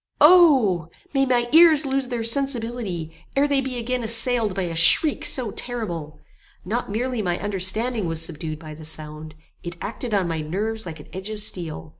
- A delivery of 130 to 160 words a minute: No, average, 180 wpm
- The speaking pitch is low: No, high, 215 Hz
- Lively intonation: Yes, wide, 6.7 semitones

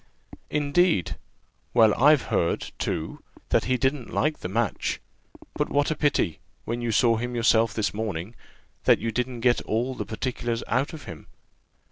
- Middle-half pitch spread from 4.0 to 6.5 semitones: No, average, 3.1 semitones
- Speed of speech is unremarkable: Yes, average, 160 wpm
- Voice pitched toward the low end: Yes, low, 120 Hz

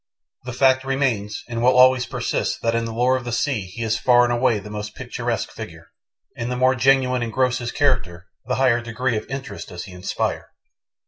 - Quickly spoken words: Yes, fast, 210 wpm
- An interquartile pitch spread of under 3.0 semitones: Yes, narrow, 2.4 semitones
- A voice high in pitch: No, low, 120 Hz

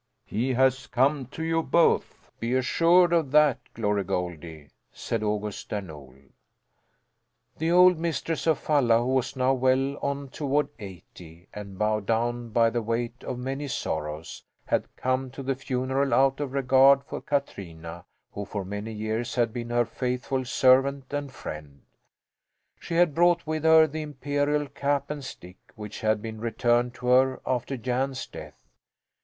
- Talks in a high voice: No, low, 130 Hz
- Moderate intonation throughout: Yes, average, 4.4 semitones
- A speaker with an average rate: Yes, average, 160 wpm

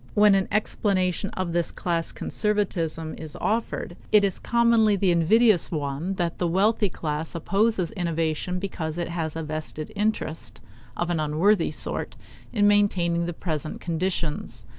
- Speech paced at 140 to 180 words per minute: Yes, average, 145 wpm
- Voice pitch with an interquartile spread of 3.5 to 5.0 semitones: Yes, average, 4.0 semitones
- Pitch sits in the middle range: Yes, medium, 175 Hz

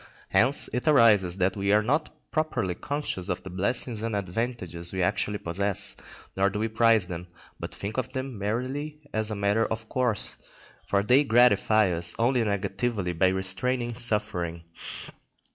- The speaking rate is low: No, average, 160 wpm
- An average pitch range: Yes, average, 4.4 semitones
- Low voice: Yes, low, 105 Hz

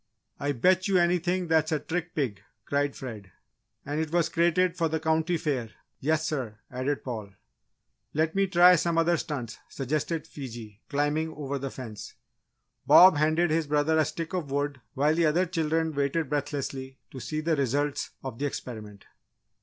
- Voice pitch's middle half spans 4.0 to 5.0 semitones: No, average, 3.4 semitones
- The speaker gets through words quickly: No, average, 170 wpm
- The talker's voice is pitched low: No, medium, 150 Hz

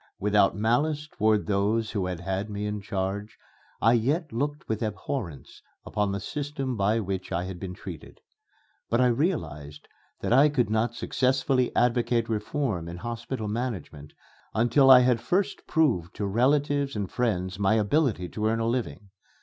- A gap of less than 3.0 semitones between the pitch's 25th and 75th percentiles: No, average, 4.6 semitones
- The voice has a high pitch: No, low, 110 Hz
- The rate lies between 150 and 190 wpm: Yes, average, 160 wpm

